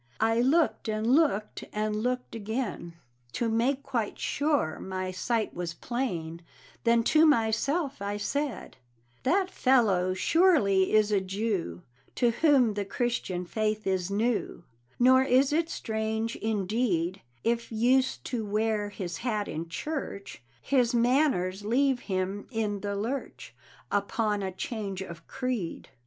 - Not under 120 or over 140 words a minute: Yes, slow, 135 wpm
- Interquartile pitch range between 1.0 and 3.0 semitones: No, average, 4.3 semitones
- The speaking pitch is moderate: No, high, 220 Hz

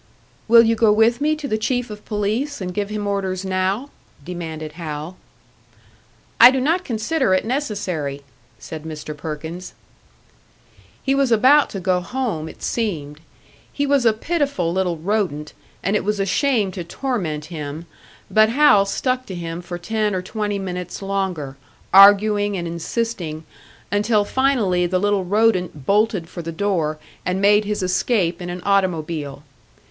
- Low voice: No, high, 195 Hz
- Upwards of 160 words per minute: No, average, 155 wpm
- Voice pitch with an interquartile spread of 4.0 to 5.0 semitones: Yes, average, 4.5 semitones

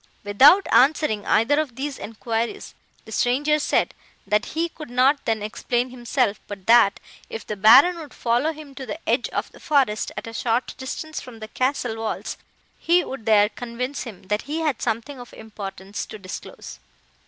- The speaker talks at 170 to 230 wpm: Yes, average, 175 wpm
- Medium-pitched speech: No, high, 240 Hz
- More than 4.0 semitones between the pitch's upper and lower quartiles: Yes, average, 4.7 semitones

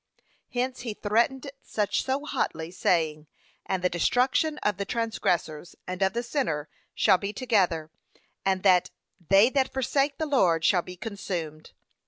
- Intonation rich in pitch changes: Yes, wide, 6.3 semitones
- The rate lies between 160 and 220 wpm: No, average, 150 wpm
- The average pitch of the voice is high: Yes, high, 200 Hz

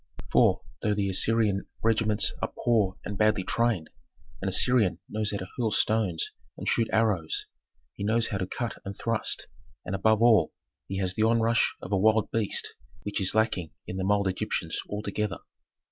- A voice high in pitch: No, low, 105 Hz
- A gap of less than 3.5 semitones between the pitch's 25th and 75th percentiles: Yes, average, 2.7 semitones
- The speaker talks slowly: No, average, 175 wpm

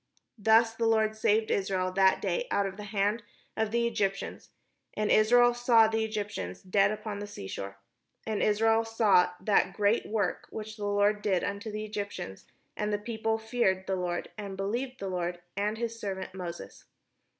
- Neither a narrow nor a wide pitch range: No, narrow, 2.2 semitones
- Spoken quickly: No, average, 175 wpm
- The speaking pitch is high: Yes, high, 210 Hz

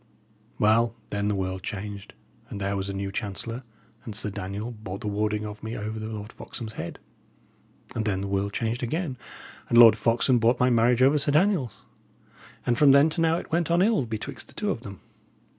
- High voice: No, low, 110 Hz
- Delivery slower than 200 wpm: No, fast, 205 wpm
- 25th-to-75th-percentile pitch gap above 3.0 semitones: Yes, average, 3.7 semitones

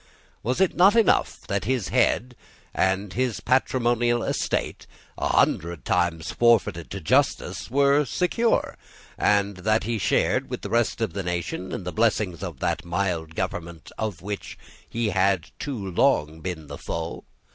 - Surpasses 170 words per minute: No, average, 150 wpm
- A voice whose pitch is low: Yes, low, 100 Hz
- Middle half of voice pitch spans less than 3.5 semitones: No, wide, 5.5 semitones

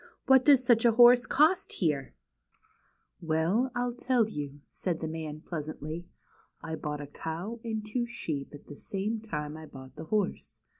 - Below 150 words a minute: No, average, 180 wpm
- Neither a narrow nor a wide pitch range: No, wide, 7.5 semitones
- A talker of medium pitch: Yes, medium, 175 Hz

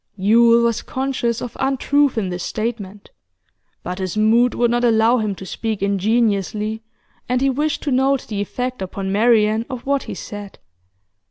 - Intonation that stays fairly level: No, average, 3.4 semitones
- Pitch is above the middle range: Yes, high, 225 Hz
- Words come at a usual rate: Yes, average, 165 wpm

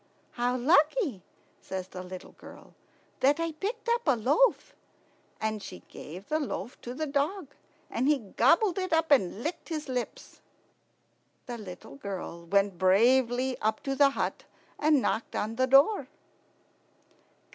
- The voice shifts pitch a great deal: Yes, wide, 6.6 semitones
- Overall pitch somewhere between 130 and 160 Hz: No, very high, 260 Hz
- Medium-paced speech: Yes, average, 145 wpm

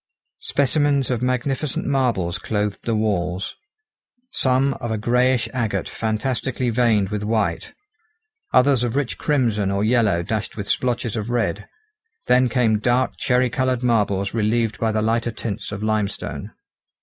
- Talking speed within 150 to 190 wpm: No, average, 140 wpm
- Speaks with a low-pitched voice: Yes, low, 115 Hz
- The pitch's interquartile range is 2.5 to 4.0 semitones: Yes, average, 3.2 semitones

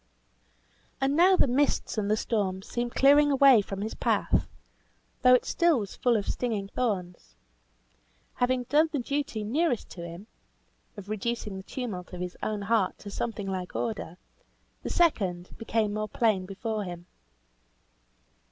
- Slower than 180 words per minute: Yes, average, 150 wpm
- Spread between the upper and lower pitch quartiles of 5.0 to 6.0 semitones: No, average, 4.5 semitones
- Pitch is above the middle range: Yes, high, 215 Hz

